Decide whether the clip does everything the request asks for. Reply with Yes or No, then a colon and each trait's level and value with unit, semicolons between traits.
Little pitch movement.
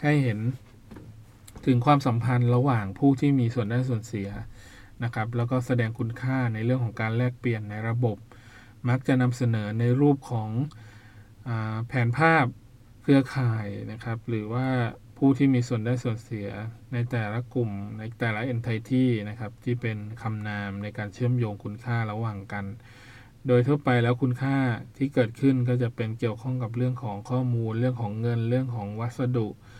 Yes: narrow, 2.3 semitones